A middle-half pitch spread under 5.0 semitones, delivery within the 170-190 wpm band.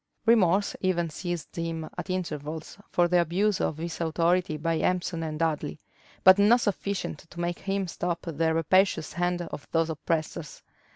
No: narrow, 2.4 semitones; average, 160 wpm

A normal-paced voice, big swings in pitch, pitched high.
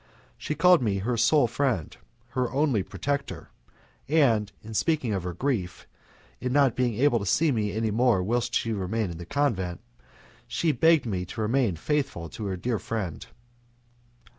No: average, 165 wpm; wide, 5.8 semitones; low, 115 Hz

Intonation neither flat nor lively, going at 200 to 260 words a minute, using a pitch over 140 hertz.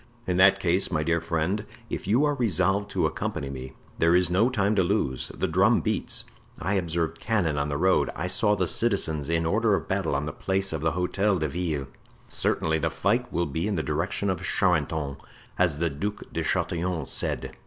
No: average, 3.9 semitones; fast, 205 wpm; very low, 90 Hz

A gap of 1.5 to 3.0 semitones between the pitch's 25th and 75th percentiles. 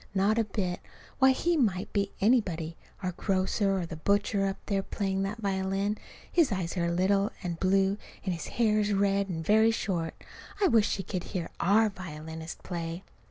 Yes: average, 2.7 semitones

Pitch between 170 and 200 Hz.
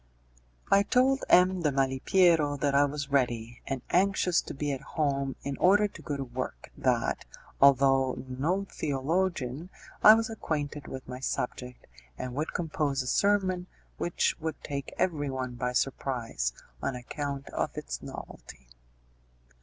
No: medium, 140 Hz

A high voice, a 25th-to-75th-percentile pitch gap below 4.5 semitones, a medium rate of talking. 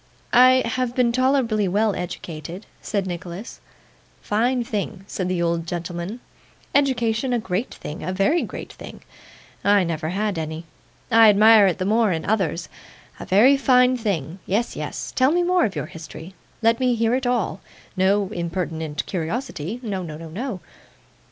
No: high, 205 Hz; wide, 5.5 semitones; average, 160 wpm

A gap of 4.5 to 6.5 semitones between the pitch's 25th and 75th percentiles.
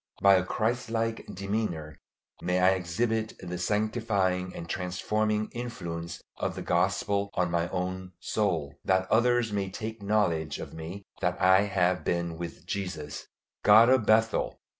No: average, 3.5 semitones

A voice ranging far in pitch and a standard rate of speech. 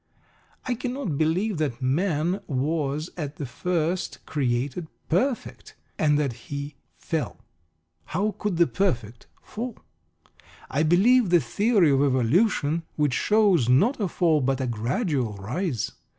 No: wide, 6.1 semitones; slow, 130 wpm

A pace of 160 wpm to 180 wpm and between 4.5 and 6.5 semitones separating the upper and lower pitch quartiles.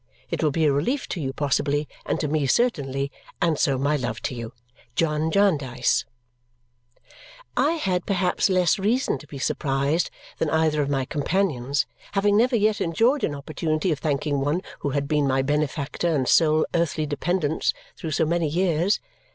No: average, 170 wpm; average, 4.0 semitones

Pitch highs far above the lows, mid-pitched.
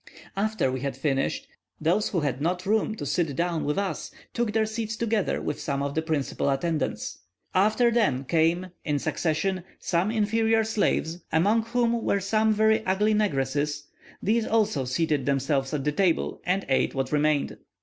Yes: wide, 6.7 semitones; medium, 175 Hz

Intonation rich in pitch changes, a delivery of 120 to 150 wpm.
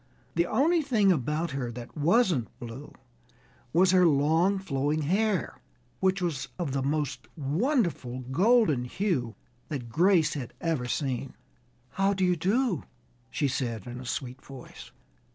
Yes: wide, 6.3 semitones; average, 140 wpm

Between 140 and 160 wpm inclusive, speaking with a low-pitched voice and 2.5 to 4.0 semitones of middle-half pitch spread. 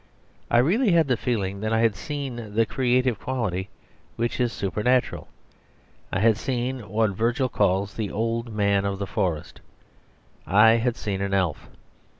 Yes: average, 155 wpm; low, 115 Hz; average, 3.7 semitones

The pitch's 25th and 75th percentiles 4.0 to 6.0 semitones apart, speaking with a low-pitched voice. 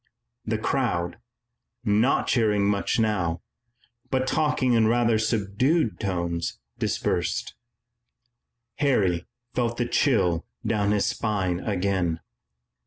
Yes: average, 4.6 semitones; low, 105 Hz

